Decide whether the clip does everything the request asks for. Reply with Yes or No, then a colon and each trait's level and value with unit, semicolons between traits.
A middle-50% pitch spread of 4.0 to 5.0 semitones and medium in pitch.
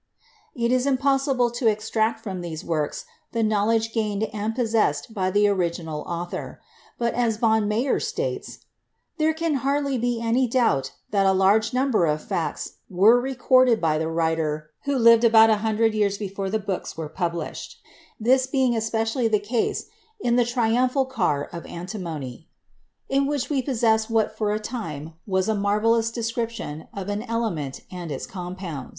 No: average, 4.4 semitones; high, 220 Hz